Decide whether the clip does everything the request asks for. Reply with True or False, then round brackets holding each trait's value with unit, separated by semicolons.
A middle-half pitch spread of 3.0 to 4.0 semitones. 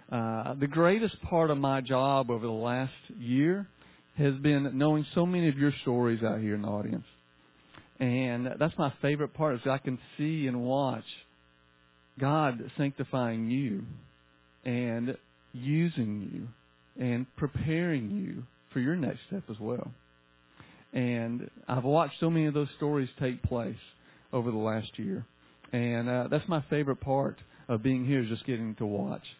False (4.6 semitones)